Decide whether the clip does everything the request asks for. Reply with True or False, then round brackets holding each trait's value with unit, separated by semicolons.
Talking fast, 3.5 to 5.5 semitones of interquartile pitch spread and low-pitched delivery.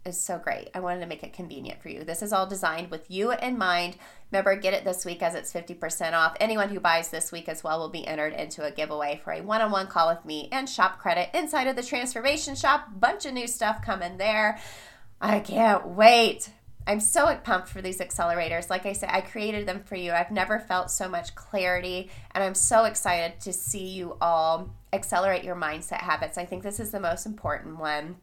False (225 wpm; 3.9 semitones; 185 Hz)